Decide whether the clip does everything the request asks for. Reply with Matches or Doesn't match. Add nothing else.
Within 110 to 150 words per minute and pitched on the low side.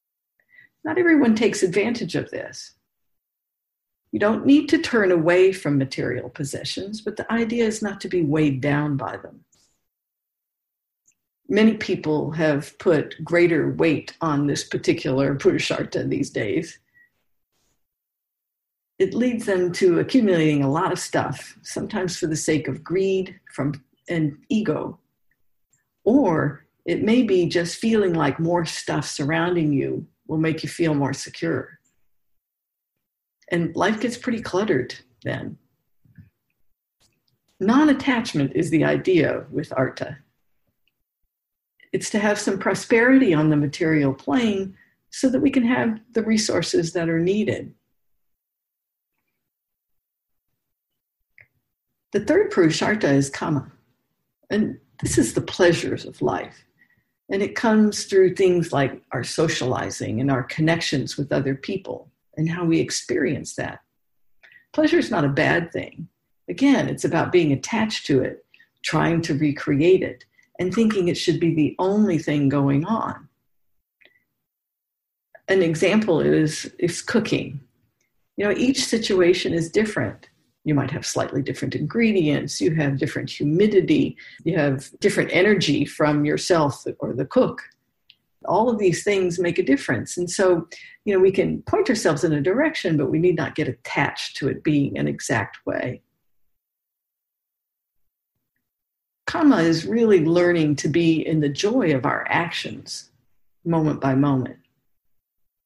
Doesn't match